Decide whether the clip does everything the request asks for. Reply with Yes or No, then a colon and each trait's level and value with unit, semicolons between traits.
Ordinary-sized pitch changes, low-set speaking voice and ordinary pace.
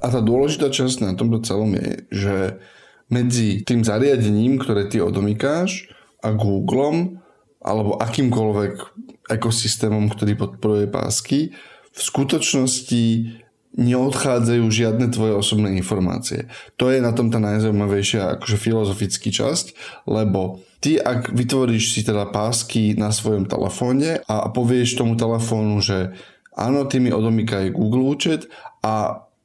Yes: average, 3.1 semitones; low, 115 Hz; average, 125 wpm